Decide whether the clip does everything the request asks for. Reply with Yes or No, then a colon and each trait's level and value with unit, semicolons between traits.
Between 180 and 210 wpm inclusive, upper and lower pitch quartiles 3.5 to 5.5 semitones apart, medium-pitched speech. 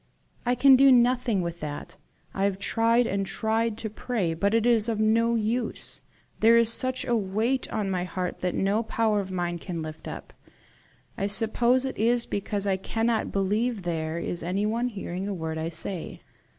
No: average, 190 wpm; average, 3.9 semitones; high, 210 Hz